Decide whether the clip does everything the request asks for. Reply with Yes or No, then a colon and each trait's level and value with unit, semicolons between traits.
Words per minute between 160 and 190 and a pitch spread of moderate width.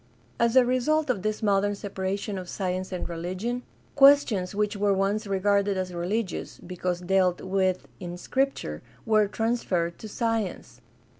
No: average, 150 wpm; average, 3.4 semitones